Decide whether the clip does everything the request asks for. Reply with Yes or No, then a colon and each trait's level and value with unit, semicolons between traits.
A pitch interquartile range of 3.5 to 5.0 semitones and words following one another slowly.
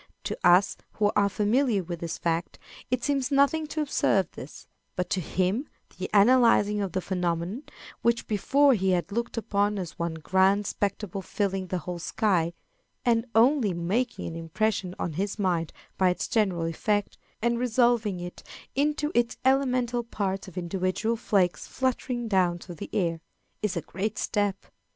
No: average, 4.7 semitones; average, 160 wpm